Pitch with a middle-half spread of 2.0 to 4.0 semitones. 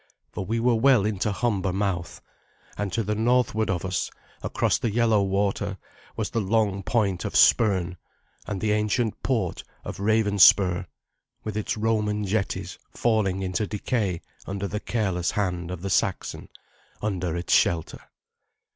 Yes: average, 2.7 semitones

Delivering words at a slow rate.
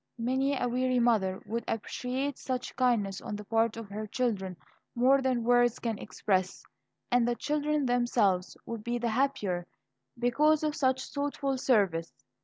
No: average, 155 wpm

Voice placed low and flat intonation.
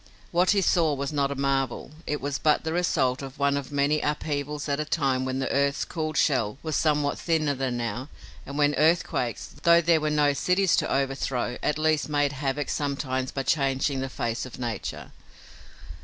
No: medium, 145 Hz; narrow, 2.3 semitones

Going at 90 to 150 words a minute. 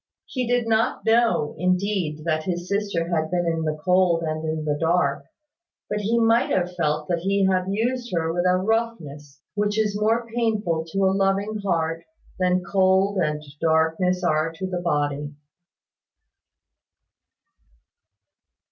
Yes: average, 145 wpm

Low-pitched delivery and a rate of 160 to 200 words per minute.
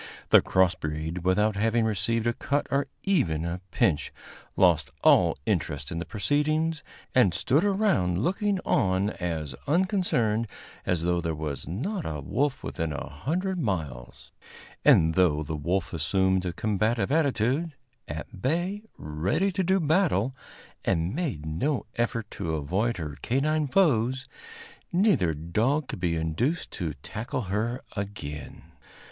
No: low, 105 Hz; average, 140 wpm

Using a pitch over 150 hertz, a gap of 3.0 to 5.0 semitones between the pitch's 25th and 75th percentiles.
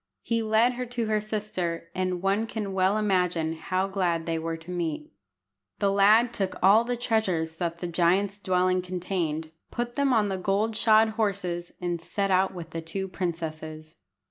Yes: medium, 185 Hz; average, 3.9 semitones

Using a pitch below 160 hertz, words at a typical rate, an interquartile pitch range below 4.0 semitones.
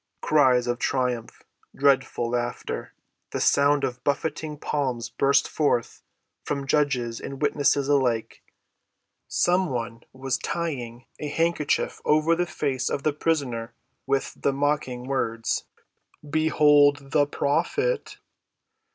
No: medium, 140 Hz; slow, 115 wpm; average, 3.3 semitones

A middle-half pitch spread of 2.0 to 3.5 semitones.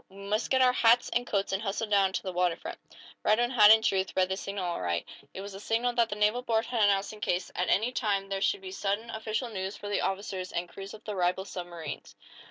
Yes: average, 2.8 semitones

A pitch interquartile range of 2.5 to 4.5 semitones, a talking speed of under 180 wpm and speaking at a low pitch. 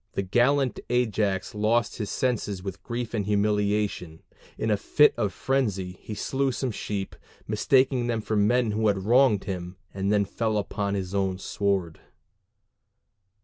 Yes: average, 3.4 semitones; average, 155 wpm; low, 105 Hz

